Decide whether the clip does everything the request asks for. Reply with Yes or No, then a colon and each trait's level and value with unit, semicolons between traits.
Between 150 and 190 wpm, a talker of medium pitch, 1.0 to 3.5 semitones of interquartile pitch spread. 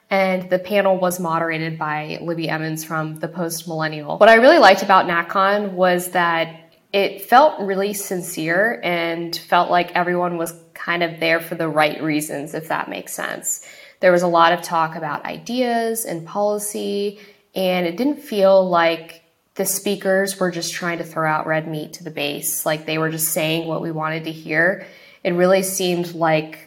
Yes: average, 185 wpm; medium, 175 Hz; average, 3.0 semitones